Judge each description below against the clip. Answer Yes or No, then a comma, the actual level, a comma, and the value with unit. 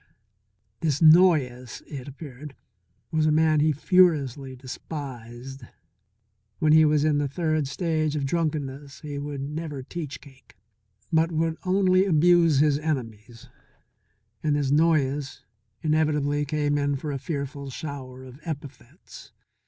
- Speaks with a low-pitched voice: No, medium, 145 Hz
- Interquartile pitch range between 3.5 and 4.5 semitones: No, narrow, 2.5 semitones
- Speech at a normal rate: No, slow, 130 wpm